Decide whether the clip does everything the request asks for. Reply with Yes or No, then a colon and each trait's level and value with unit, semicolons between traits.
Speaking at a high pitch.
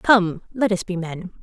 Yes: high, 195 Hz